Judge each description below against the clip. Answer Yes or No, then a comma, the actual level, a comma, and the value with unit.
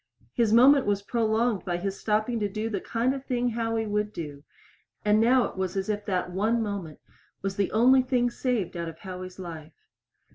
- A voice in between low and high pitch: No, high, 210 Hz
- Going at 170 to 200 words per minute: Yes, average, 195 wpm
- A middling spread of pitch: Yes, average, 3.8 semitones